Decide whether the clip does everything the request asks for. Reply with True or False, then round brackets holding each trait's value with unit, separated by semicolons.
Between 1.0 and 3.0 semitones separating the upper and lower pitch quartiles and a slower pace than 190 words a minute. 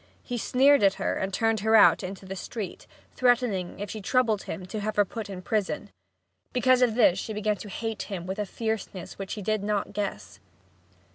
False (2.7 semitones; 205 wpm)